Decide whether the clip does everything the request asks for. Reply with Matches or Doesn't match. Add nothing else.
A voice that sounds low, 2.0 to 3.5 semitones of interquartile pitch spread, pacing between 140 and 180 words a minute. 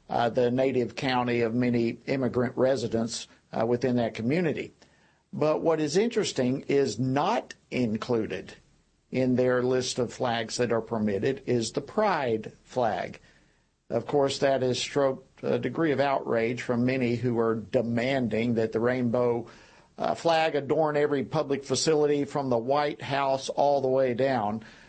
Matches